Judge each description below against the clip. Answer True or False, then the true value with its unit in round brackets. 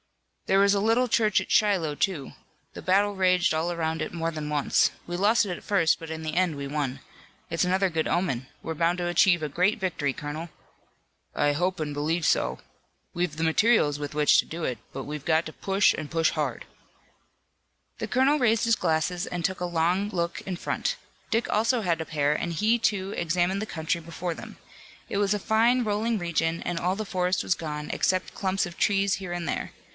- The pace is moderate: False (210 wpm)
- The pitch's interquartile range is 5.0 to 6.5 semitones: False (3.7 semitones)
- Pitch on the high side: False (175 Hz)